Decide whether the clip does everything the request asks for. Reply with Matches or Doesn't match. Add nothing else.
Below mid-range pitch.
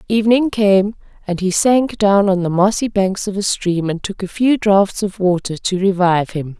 Doesn't match